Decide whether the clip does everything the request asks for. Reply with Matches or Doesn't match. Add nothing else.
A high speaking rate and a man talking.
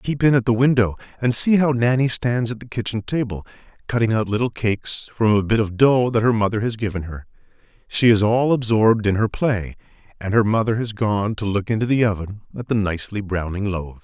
Matches